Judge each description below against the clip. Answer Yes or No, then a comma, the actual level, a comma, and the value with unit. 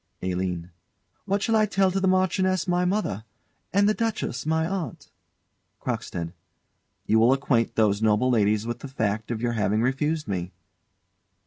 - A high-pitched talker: No, low, 130 Hz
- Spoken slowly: No, average, 155 wpm